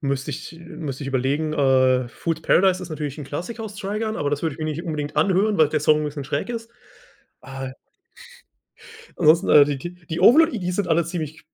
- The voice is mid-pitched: Yes, medium, 155 Hz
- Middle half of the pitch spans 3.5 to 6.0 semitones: Yes, average, 4.1 semitones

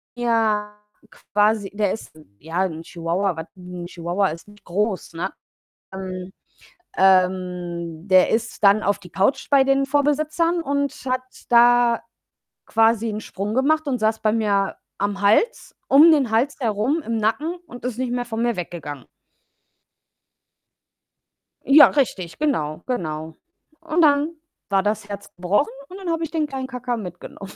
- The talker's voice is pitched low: No, high, 215 Hz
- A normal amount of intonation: No, wide, 6.2 semitones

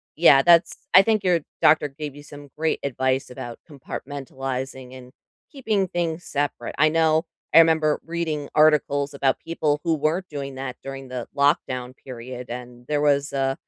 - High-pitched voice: No, medium, 145 Hz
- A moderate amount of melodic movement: Yes, average, 3.3 semitones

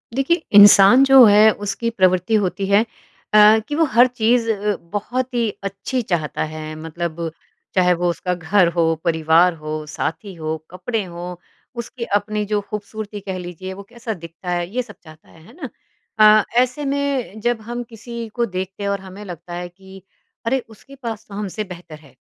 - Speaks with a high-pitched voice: Yes, high, 200 Hz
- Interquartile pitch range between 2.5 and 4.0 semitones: No, average, 4.6 semitones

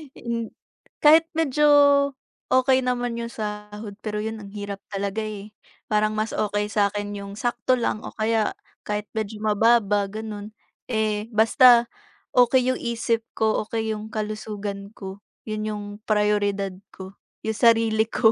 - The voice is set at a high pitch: Yes, high, 215 Hz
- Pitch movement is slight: Yes, narrow, 1.8 semitones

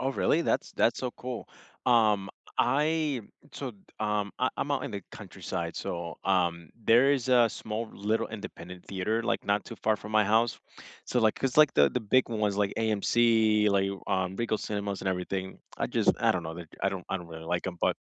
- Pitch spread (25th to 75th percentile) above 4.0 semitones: No, average, 3.6 semitones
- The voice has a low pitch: Yes, low, 105 Hz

